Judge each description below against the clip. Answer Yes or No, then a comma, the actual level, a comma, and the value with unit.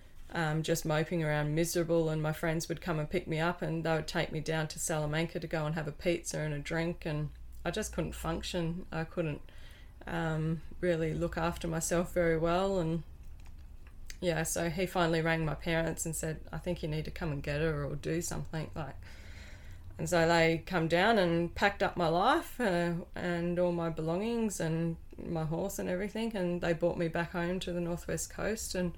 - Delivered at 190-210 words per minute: Yes, fast, 205 wpm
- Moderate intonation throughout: No, narrow, 1.7 semitones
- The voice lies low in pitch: No, medium, 165 Hz